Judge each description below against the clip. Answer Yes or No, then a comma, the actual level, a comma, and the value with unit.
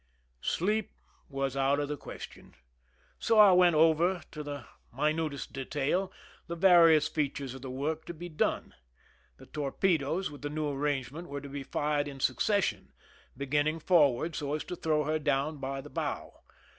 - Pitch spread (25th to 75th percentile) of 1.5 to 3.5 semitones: Yes, average, 2.9 semitones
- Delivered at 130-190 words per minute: Yes, average, 175 wpm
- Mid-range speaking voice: Yes, medium, 150 Hz